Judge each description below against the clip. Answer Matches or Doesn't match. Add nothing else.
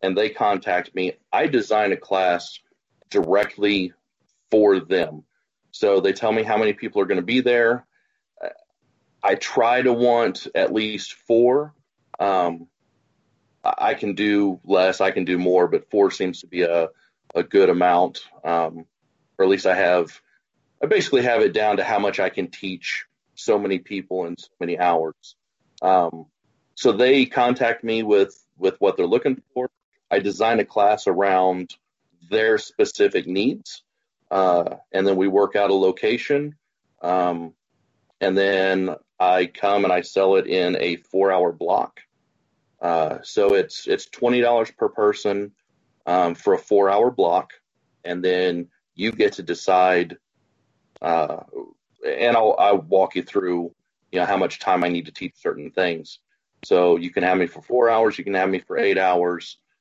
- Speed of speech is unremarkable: Matches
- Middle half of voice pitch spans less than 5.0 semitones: Doesn't match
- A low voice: Matches